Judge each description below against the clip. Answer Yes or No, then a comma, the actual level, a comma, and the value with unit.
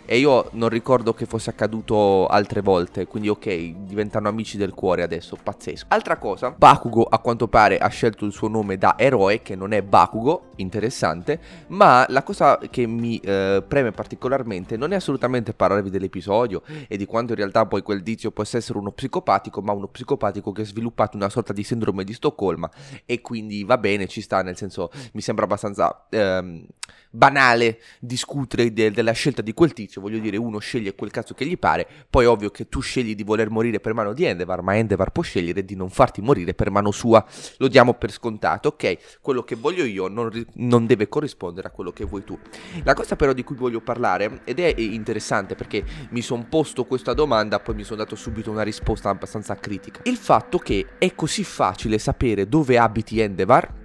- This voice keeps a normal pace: No, fast, 200 wpm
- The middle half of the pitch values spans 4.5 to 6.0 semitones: No, average, 2.8 semitones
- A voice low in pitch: Yes, low, 110 Hz